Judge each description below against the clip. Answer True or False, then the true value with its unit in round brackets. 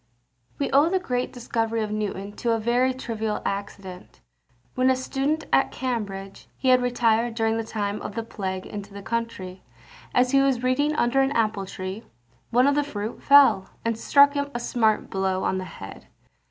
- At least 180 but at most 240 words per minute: True (185 wpm)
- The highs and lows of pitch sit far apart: False (4.1 semitones)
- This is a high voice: True (230 Hz)